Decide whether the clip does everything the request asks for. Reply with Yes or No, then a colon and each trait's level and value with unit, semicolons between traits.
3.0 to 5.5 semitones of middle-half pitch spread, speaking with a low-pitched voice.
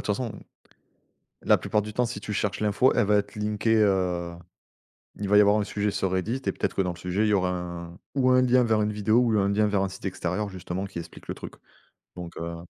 No: narrow, 2.6 semitones; low, 100 Hz